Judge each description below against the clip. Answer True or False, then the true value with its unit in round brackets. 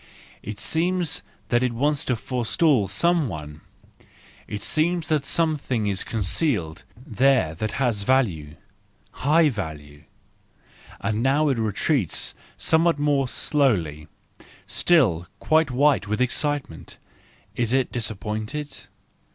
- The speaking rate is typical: False (110 wpm)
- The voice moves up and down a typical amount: False (6.4 semitones)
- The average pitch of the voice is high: False (125 Hz)